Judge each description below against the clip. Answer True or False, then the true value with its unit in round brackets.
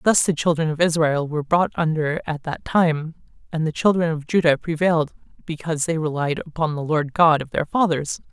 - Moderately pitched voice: True (160 Hz)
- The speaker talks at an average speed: True (195 wpm)